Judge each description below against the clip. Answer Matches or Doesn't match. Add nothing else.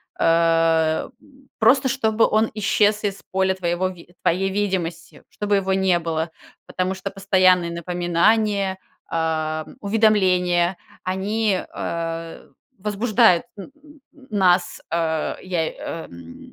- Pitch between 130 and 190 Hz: Matches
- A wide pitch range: Doesn't match